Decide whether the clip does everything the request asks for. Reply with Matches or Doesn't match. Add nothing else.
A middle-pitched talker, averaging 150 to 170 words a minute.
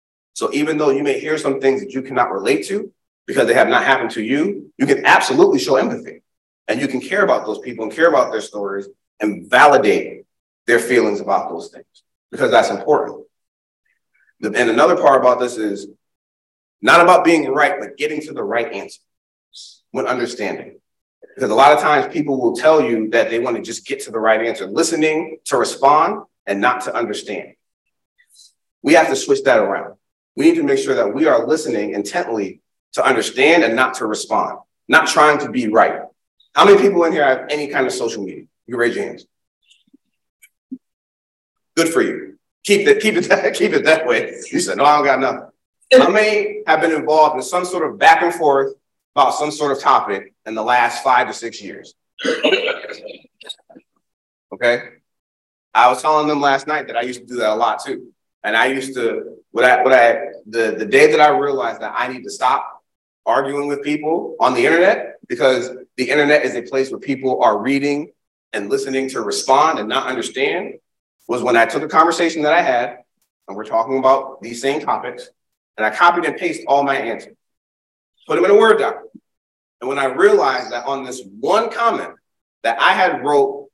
Doesn't match